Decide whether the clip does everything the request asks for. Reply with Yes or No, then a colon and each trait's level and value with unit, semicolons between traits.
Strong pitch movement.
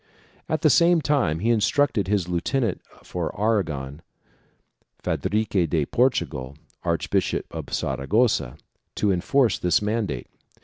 Yes: wide, 6.7 semitones